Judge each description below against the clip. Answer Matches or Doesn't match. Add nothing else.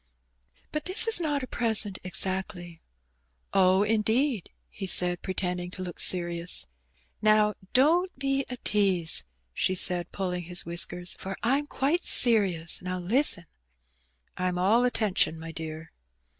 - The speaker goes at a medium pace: Doesn't match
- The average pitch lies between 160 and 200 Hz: Matches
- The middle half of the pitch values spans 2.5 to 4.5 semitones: Doesn't match